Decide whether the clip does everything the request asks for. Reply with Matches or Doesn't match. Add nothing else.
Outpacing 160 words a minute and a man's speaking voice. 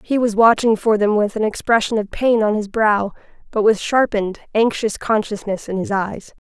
Doesn't match